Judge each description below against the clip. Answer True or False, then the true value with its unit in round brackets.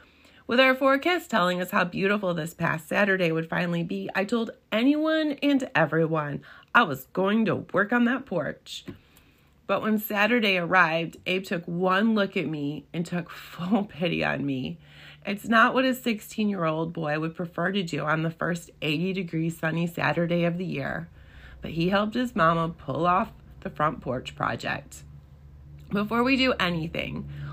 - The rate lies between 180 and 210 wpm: False (165 wpm)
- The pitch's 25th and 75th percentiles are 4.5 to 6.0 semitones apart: True (4.8 semitones)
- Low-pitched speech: False (180 Hz)